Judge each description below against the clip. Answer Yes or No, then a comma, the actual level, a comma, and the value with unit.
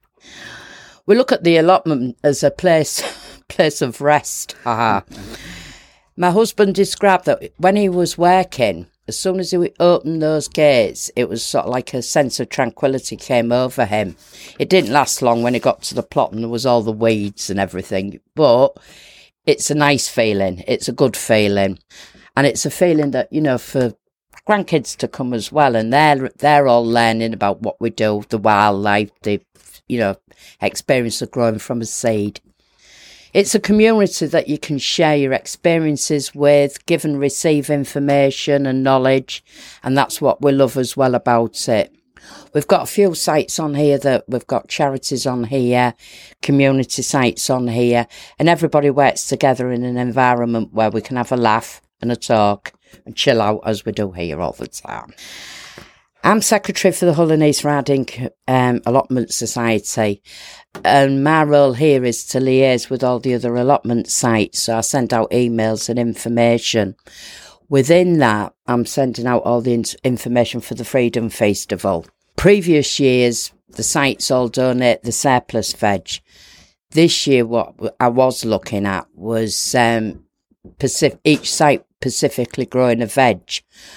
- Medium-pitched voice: No, low, 125 Hz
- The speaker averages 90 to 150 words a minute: No, average, 170 wpm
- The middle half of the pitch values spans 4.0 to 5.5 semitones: Yes, average, 4.3 semitones